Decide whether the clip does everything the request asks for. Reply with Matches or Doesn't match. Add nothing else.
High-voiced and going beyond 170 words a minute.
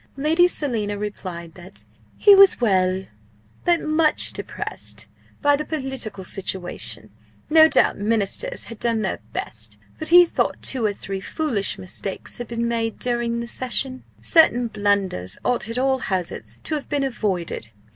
Doesn't match